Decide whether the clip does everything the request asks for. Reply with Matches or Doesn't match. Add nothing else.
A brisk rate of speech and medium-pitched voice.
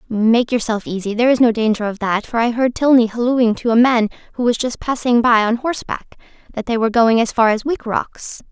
Doesn't match